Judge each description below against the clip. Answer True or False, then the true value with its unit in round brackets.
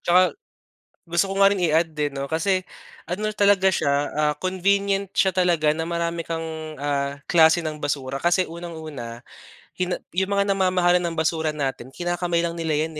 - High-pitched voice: False (170 Hz)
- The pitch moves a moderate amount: True (3.0 semitones)